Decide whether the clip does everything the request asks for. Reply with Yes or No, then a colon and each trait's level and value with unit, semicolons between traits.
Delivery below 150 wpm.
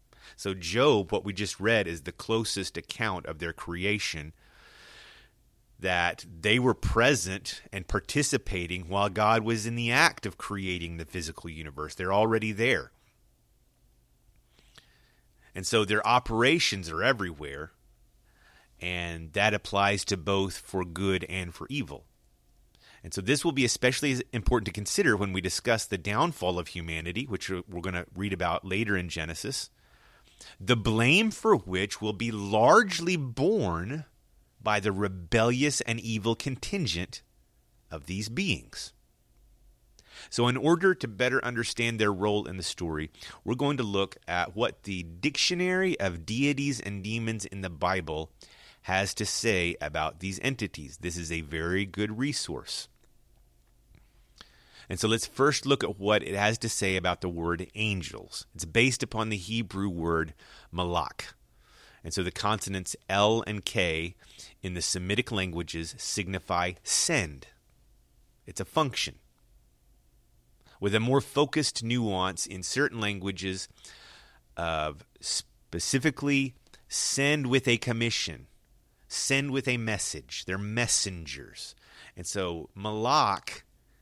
Yes: slow, 135 wpm